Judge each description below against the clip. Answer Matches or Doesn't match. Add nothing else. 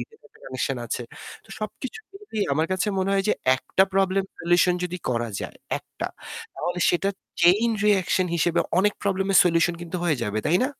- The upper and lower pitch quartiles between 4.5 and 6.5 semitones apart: Doesn't match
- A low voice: Doesn't match